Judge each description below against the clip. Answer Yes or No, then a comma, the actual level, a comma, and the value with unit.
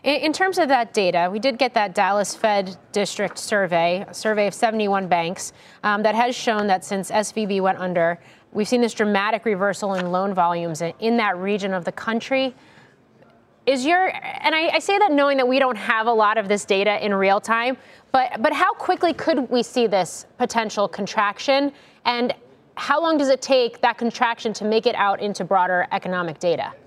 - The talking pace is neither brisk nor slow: Yes, average, 195 wpm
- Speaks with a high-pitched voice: Yes, high, 215 Hz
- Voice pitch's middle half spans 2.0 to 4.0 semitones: No, average, 5.0 semitones